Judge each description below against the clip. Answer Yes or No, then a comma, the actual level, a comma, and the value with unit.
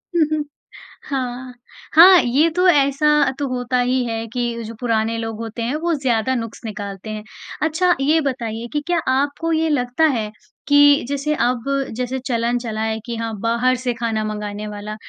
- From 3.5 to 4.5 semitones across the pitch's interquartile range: Yes, average, 4.0 semitones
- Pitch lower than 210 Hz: No, high, 245 Hz